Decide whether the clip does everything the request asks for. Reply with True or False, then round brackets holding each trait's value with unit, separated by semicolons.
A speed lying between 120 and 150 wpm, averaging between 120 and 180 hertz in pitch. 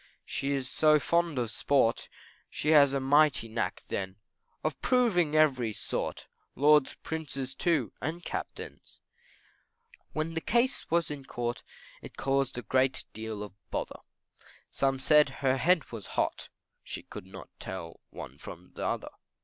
True (145 wpm; 140 Hz)